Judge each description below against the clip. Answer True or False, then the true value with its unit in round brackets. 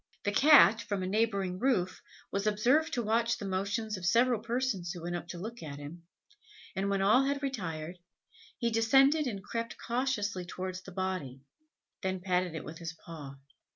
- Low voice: False (200 Hz)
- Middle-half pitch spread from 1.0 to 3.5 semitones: False (4.6 semitones)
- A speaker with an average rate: True (180 wpm)